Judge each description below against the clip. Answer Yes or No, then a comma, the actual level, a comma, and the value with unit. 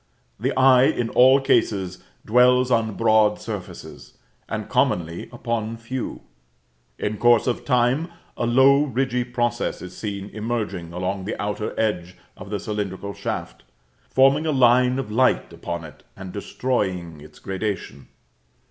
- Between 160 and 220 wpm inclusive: No, average, 140 wpm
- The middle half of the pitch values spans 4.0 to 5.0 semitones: Yes, average, 4.5 semitones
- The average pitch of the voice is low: Yes, low, 110 Hz